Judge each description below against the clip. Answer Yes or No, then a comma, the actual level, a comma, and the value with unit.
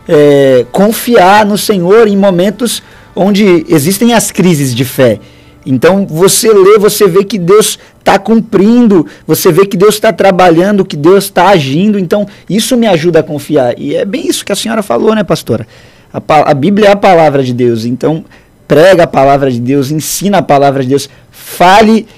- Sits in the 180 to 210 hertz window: Yes, high, 190 Hz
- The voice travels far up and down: Yes, wide, 6.2 semitones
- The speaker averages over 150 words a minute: Yes, average, 180 wpm